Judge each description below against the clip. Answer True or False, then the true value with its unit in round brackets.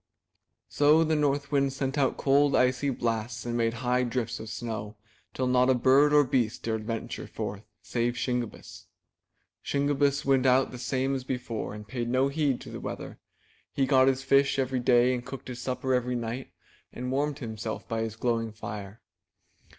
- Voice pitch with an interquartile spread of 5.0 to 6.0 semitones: False (2.6 semitones)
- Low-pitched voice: True (125 Hz)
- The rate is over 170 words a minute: True (180 wpm)